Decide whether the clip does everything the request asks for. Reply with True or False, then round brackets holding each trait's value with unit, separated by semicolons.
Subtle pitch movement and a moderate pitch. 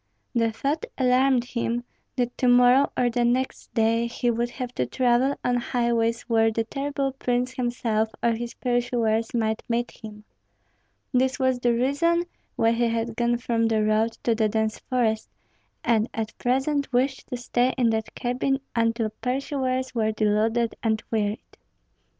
False (2.0 semitones; 240 Hz)